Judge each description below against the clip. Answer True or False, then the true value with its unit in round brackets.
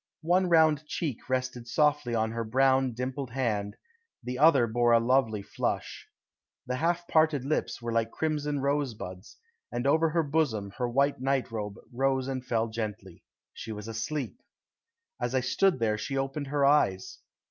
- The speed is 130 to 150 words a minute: False (160 wpm)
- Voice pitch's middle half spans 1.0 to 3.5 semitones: False (4.1 semitones)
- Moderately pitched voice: False (130 Hz)